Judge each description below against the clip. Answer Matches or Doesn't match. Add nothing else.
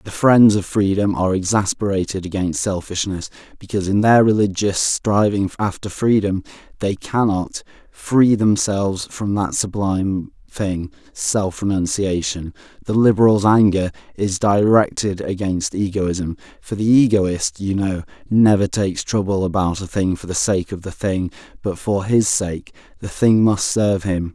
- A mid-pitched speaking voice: Doesn't match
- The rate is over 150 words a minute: Doesn't match